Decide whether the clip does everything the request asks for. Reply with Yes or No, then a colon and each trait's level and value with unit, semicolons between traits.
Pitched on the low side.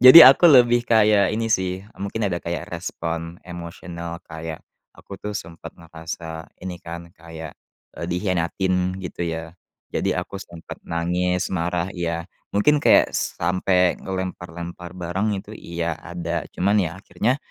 Yes: very low, 90 Hz